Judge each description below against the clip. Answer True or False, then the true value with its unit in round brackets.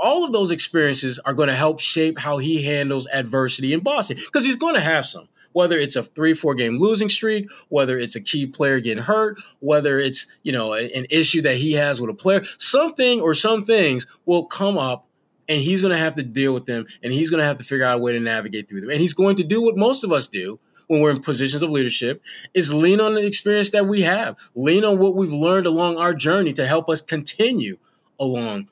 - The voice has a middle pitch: True (160 Hz)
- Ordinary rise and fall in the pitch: False (6.2 semitones)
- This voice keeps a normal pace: False (240 wpm)